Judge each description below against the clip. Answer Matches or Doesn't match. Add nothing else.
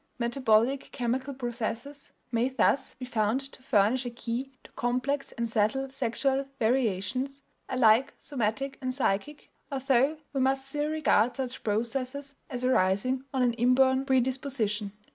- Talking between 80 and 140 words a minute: Matches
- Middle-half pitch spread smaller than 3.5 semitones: Matches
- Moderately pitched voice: Doesn't match